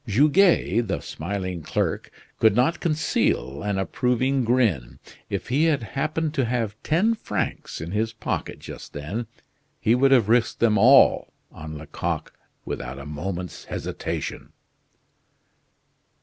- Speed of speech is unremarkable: No, slow, 130 wpm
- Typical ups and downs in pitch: No, wide, 6.8 semitones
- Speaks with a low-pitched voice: Yes, low, 115 Hz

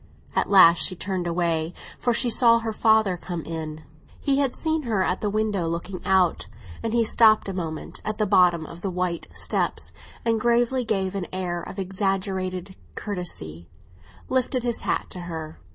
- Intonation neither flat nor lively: Yes, average, 4.1 semitones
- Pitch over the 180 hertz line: Yes, high, 190 Hz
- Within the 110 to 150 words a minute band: No, average, 175 wpm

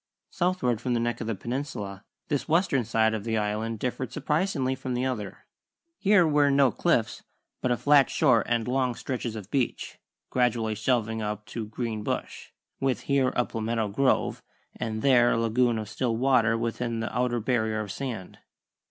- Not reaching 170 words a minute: No, average, 175 wpm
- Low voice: Yes, low, 120 Hz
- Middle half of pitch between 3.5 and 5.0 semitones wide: No, average, 2.9 semitones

